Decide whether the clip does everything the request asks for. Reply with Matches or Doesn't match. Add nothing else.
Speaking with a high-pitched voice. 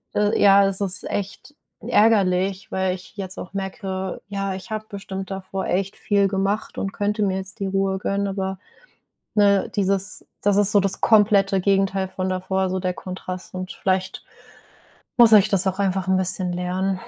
Matches